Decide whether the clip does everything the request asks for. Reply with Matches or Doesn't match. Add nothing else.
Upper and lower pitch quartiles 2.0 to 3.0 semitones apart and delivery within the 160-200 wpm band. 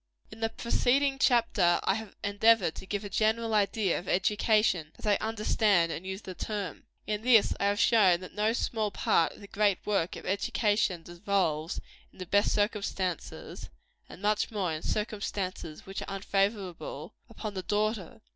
Matches